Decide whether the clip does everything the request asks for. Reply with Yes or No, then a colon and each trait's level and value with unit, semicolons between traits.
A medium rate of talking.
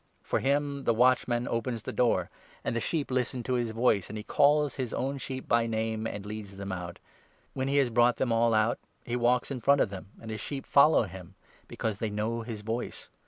No: fast, 230 wpm